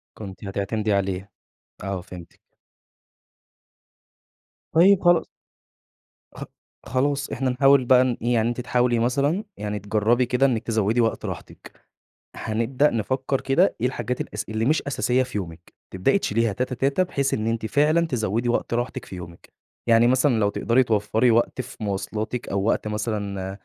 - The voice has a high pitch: No, low, 115 Hz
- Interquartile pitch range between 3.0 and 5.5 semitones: Yes, average, 3.7 semitones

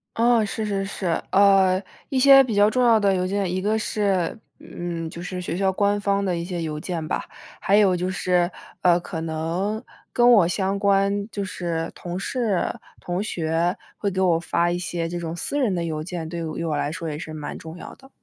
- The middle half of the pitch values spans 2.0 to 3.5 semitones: Yes, average, 3.1 semitones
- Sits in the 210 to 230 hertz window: No, medium, 185 Hz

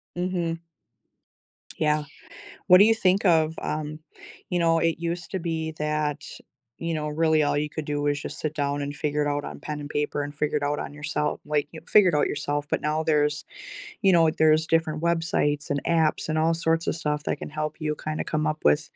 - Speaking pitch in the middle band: Yes, medium, 155 Hz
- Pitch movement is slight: Yes, narrow, 1.8 semitones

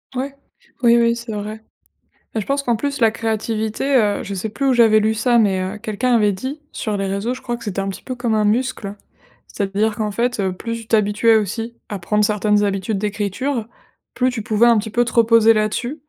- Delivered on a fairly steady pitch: Yes, narrow, 2.3 semitones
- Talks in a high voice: Yes, high, 220 Hz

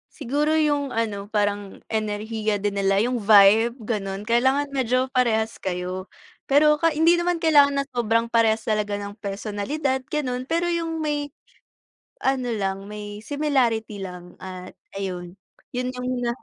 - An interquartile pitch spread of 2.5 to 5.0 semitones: No, wide, 5.4 semitones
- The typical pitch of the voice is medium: No, high, 230 Hz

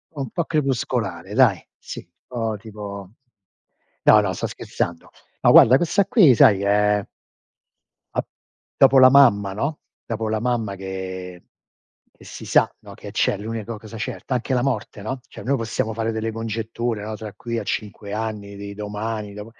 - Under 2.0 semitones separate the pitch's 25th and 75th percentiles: No, average, 2.7 semitones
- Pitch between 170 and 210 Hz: No, low, 110 Hz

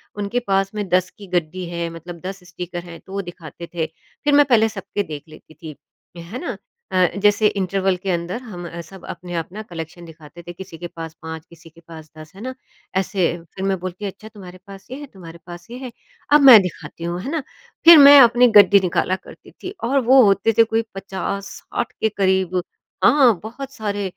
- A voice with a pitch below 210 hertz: Yes, high, 190 Hz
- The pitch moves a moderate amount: Yes, average, 4.1 semitones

